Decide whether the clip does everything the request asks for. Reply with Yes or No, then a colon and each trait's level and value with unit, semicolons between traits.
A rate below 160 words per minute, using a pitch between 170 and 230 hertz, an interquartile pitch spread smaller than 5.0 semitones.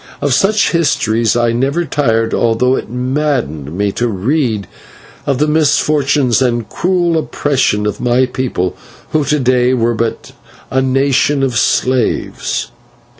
No: slow, 135 wpm; low, 130 Hz; average, 4.0 semitones